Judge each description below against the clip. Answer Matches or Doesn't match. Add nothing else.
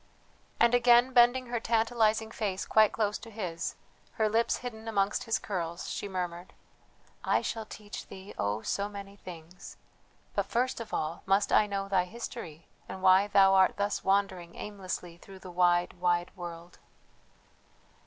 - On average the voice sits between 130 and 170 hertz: Doesn't match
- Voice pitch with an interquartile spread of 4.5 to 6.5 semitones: Doesn't match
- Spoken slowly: Doesn't match